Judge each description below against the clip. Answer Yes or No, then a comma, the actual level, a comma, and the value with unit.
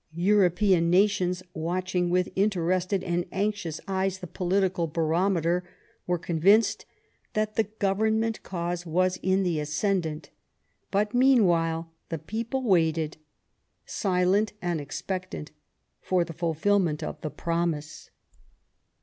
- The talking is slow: Yes, slow, 110 wpm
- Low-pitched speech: No, medium, 180 Hz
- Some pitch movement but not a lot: Yes, average, 3.1 semitones